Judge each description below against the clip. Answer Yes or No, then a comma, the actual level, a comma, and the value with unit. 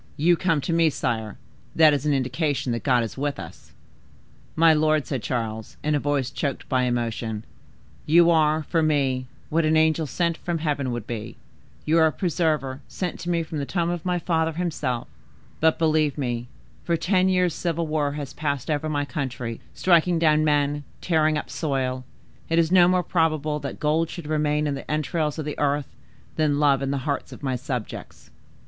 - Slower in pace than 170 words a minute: No, average, 190 wpm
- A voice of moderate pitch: Yes, medium, 150 Hz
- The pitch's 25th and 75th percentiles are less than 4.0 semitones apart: Yes, average, 3.0 semitones